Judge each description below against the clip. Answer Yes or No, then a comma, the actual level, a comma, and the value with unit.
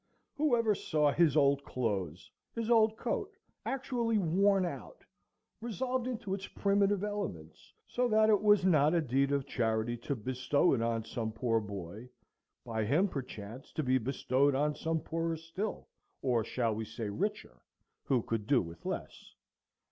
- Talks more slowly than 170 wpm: Yes, average, 155 wpm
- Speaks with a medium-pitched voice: Yes, medium, 145 Hz